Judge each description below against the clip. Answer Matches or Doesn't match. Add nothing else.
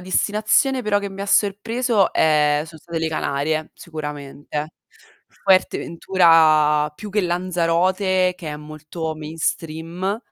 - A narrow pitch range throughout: Doesn't match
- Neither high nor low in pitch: Matches